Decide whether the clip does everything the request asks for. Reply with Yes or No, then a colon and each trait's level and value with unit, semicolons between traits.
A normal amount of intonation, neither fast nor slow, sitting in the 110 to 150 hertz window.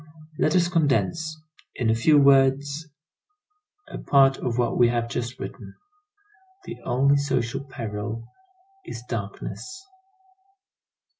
No: average, 3.9 semitones; slow, 115 wpm; low, 135 Hz